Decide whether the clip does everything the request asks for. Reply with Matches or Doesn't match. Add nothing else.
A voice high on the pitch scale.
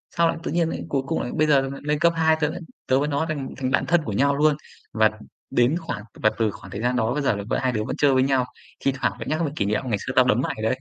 Doesn't match